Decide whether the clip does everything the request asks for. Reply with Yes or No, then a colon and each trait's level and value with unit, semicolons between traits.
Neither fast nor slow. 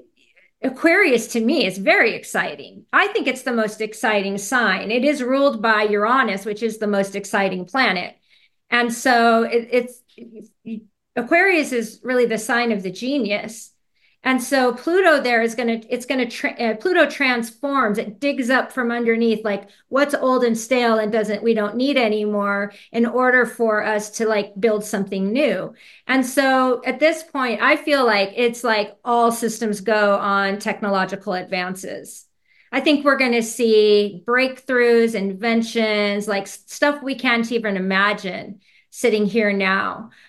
Yes: average, 160 wpm